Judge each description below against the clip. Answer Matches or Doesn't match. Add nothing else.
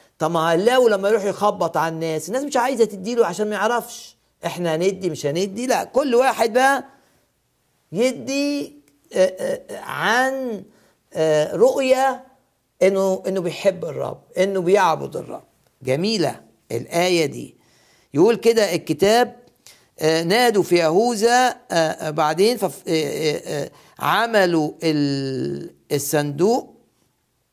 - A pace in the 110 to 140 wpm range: Doesn't match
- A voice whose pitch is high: Matches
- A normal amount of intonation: Doesn't match